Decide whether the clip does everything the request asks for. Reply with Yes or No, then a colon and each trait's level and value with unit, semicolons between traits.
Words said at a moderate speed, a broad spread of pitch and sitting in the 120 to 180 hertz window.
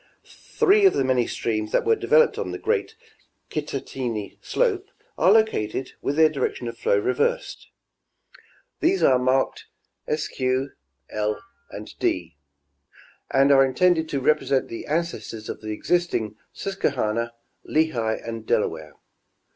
No: slow, 130 wpm; wide, 7.9 semitones; low, 135 Hz